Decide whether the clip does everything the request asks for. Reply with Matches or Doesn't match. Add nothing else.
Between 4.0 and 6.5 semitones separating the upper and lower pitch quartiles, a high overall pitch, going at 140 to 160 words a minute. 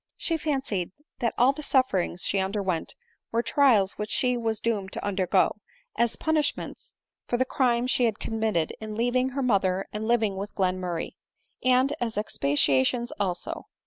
Matches